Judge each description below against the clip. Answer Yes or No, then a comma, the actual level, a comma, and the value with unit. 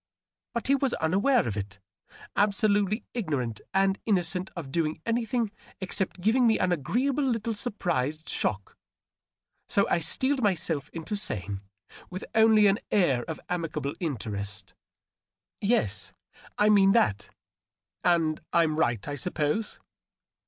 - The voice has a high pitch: No, medium, 180 Hz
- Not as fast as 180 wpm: Yes, average, 140 wpm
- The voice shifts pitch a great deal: Yes, wide, 6.9 semitones